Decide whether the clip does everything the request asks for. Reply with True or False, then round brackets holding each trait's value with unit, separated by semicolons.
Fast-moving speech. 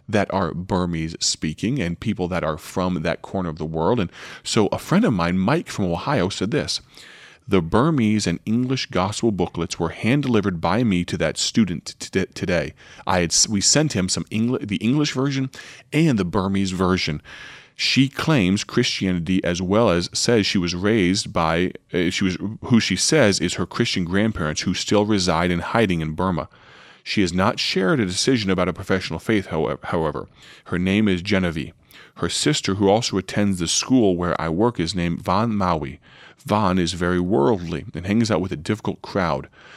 False (185 wpm)